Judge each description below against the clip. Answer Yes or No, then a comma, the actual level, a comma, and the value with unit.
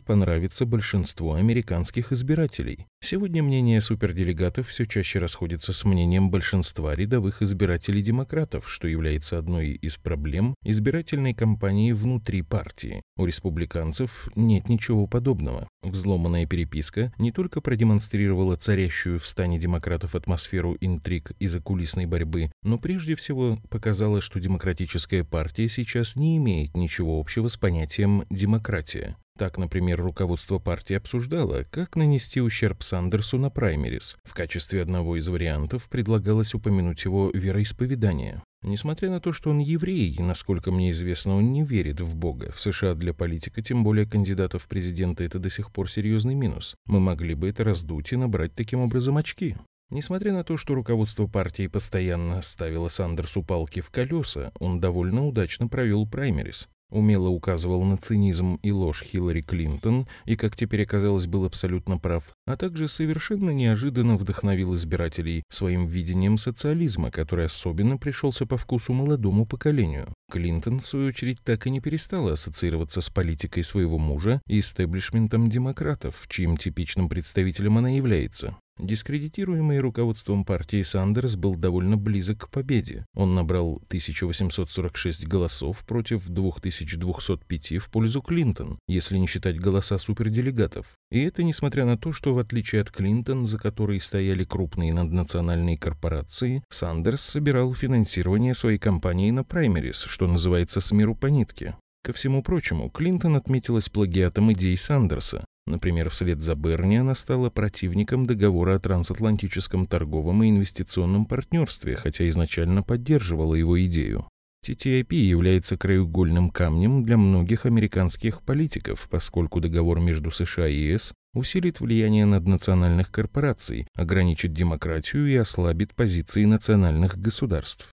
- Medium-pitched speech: No, low, 100 Hz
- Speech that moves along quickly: No, average, 135 wpm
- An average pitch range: Yes, average, 4.9 semitones